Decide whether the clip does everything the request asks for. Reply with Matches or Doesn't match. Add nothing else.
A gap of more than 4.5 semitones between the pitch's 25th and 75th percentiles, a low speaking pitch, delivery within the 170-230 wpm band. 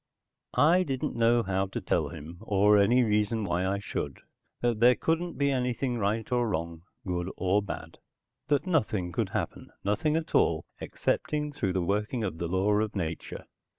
Matches